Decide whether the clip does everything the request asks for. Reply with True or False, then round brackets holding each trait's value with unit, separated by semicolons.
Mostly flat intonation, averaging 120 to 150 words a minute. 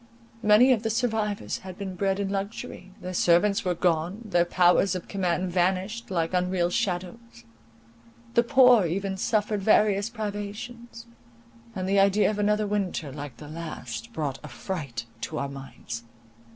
False (3.3 semitones; 145 wpm)